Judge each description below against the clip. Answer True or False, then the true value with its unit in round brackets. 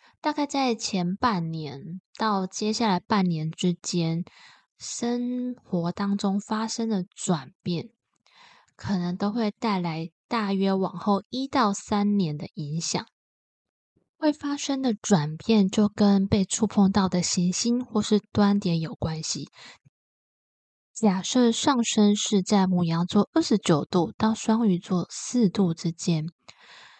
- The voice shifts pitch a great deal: False (4.0 semitones)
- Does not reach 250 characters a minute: True (185 characters per minute)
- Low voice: False (200 Hz)